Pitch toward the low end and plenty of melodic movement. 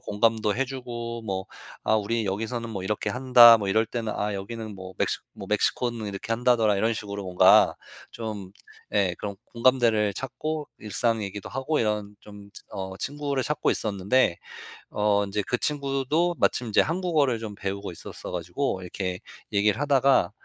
No: low, 110 Hz; average, 3.9 semitones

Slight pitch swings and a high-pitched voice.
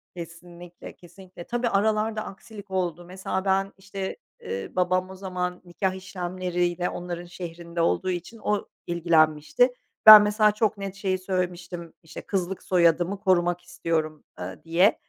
No: narrow, 2.0 semitones; medium, 180 Hz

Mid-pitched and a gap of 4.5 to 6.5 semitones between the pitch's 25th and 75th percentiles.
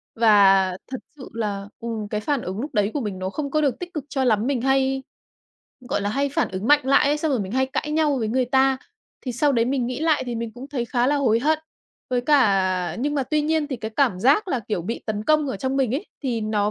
No: very high, 255 Hz; average, 4.8 semitones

